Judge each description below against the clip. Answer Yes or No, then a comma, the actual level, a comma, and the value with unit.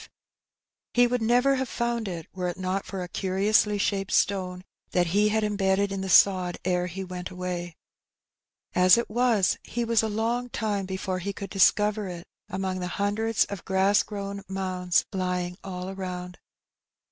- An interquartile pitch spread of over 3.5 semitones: No, narrow, 2.5 semitones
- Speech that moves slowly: No, average, 170 wpm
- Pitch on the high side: Yes, high, 195 Hz